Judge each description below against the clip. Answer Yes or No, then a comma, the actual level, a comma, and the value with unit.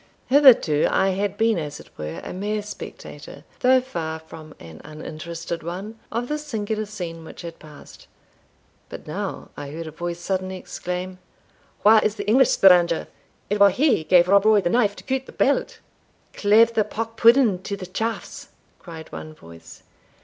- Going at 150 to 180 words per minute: Yes, average, 170 wpm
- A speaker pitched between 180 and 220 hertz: Yes, high, 190 Hz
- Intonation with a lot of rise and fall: No, average, 4.9 semitones